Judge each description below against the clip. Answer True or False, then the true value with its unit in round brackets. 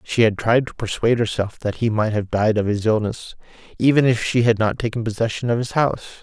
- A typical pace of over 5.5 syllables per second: True (6.0 syllables/s)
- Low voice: True (115 Hz)